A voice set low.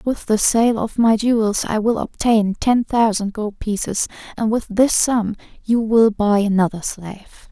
No: high, 220 Hz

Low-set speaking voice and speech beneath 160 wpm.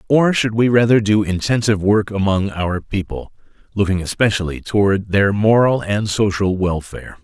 Yes: low, 105 Hz; average, 150 wpm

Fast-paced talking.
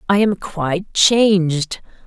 No: slow, 115 wpm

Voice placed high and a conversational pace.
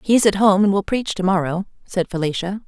No: high, 195 Hz; fast, 225 wpm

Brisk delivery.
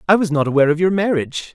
Yes: fast, 270 wpm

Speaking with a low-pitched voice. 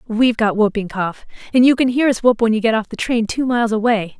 No: high, 230 Hz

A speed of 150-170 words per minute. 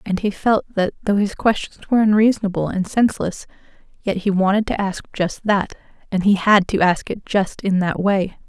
No: average, 200 wpm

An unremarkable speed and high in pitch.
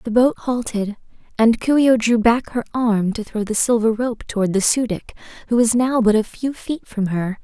No: fast, 235 wpm; high, 230 Hz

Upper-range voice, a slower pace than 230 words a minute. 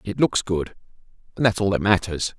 No: low, 100 Hz; average, 200 wpm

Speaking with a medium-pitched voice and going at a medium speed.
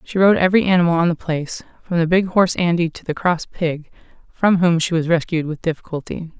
No: medium, 170 Hz; fast, 215 wpm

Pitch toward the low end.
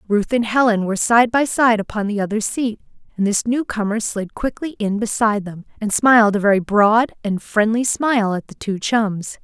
No: high, 215 Hz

